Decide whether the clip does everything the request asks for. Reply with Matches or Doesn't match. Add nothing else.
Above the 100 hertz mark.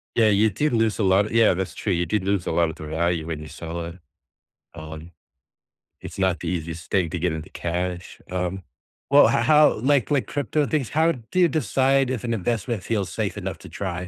Doesn't match